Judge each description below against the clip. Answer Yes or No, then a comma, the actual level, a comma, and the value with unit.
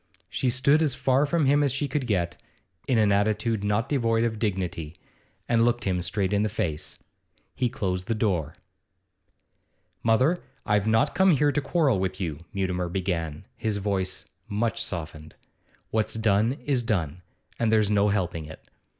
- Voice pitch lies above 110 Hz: No, low, 105 Hz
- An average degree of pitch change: Yes, average, 4.6 semitones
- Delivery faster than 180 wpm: No, average, 165 wpm